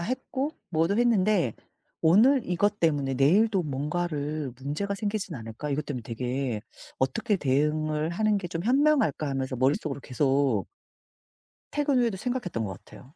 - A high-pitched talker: No, medium, 155 Hz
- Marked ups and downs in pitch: Yes, wide, 7.2 semitones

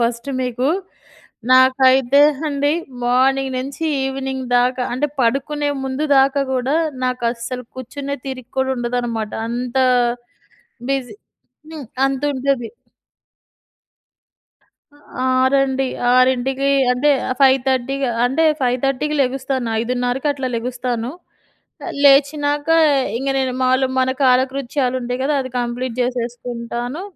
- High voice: Yes, very high, 260 Hz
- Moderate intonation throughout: No, narrow, 1.7 semitones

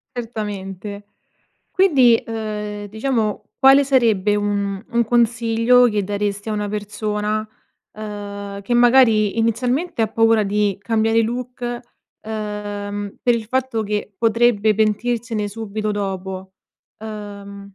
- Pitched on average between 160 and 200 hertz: No, high, 215 Hz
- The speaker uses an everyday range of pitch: No, narrow, 2.2 semitones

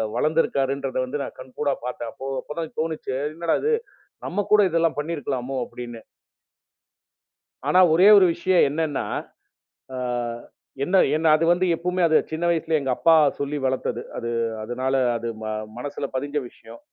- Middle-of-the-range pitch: Yes, medium, 150 Hz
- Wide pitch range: No, average, 4.1 semitones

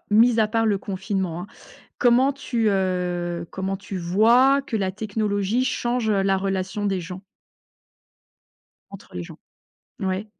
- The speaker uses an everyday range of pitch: Yes, average, 3.1 semitones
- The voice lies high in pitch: Yes, high, 200 Hz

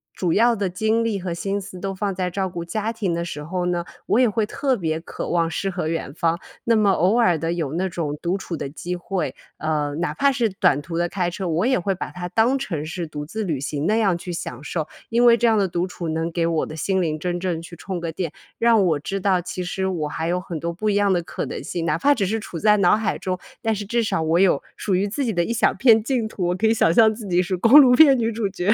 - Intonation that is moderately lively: Yes, average, 4.2 semitones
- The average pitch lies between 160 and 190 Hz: Yes, medium, 185 Hz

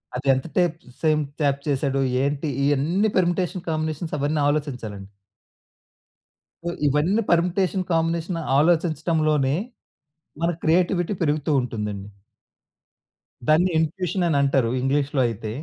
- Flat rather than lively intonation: No, average, 3.7 semitones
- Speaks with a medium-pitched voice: Yes, medium, 155 Hz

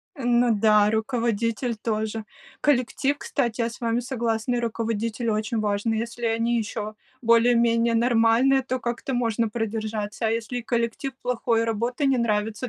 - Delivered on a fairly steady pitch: Yes, narrow, 1.5 semitones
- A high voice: Yes, high, 230 Hz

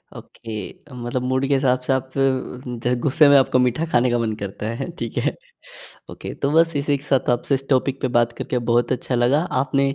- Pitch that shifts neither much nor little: No, narrow, 2.3 semitones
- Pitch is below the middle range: Yes, low, 130 Hz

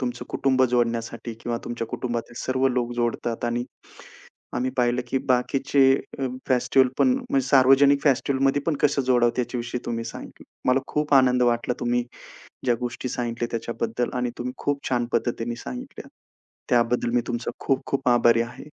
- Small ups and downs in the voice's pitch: Yes, narrow, 2.0 semitones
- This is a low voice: Yes, low, 125 Hz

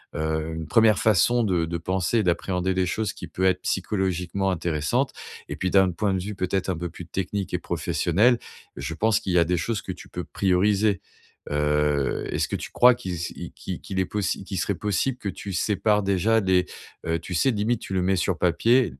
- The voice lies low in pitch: Yes, very low, 95 Hz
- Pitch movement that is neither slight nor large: Yes, average, 3.3 semitones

